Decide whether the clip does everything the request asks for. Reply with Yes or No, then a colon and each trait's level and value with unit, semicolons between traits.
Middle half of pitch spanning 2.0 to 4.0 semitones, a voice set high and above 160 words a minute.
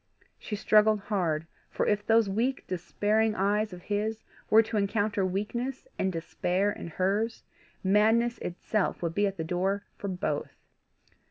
No: average, 2.7 semitones; high, 205 Hz; average, 150 wpm